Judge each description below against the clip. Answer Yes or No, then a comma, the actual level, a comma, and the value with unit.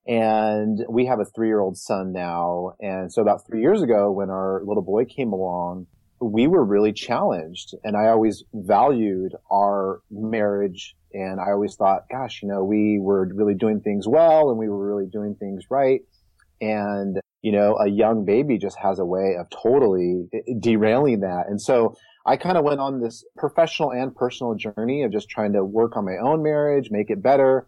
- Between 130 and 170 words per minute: No, average, 195 wpm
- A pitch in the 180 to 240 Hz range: No, low, 105 Hz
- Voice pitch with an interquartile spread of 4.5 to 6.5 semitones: No, average, 2.9 semitones